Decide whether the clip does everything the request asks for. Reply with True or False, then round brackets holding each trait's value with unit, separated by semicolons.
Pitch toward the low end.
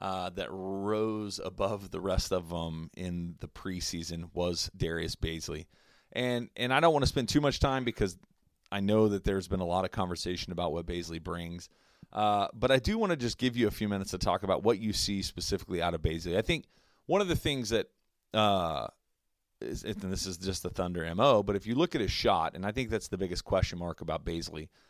True (95 Hz)